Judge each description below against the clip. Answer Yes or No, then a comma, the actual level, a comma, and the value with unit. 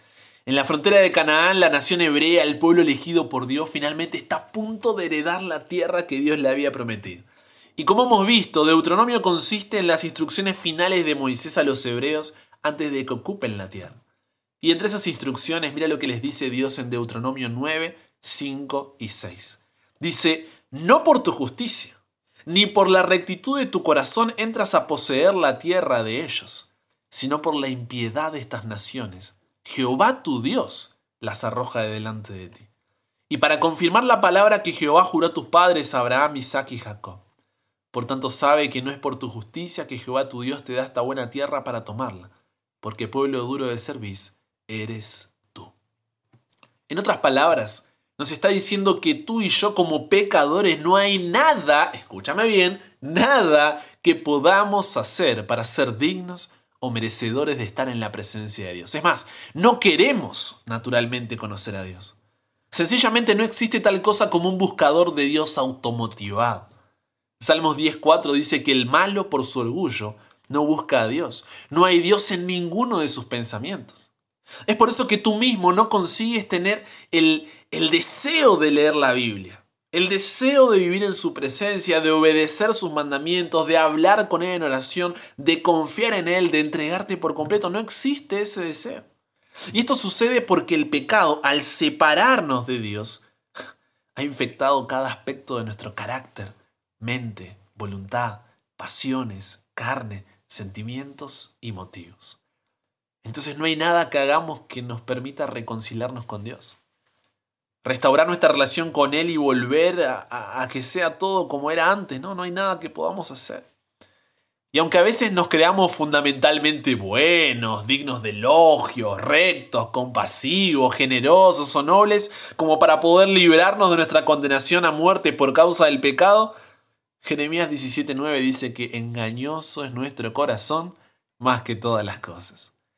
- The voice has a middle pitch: Yes, medium, 145 Hz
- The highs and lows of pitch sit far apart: Yes, wide, 6.6 semitones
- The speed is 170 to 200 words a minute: No, average, 160 wpm